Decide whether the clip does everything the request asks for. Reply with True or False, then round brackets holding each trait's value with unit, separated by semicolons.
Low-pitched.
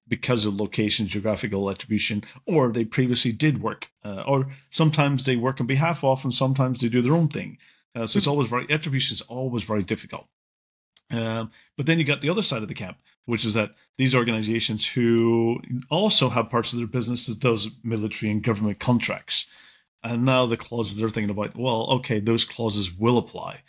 True (120 Hz)